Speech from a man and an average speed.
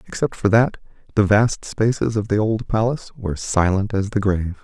Yes: male; average, 195 wpm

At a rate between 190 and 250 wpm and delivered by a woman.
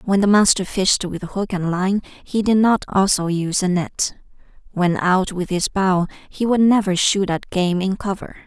Yes: average, 200 wpm; female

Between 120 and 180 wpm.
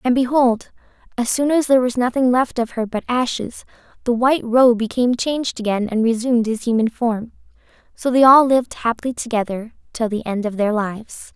No: average, 190 wpm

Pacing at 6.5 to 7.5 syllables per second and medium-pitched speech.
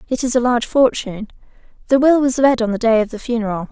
No: 6.9 syllables/s; high, 235 Hz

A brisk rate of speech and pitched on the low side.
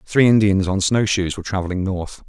Yes: fast, 210 wpm; low, 100 Hz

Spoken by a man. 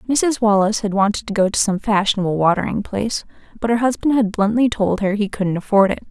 No: female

